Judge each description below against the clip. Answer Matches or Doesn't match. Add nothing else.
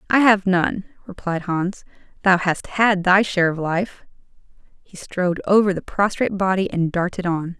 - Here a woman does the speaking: Matches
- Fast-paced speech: Doesn't match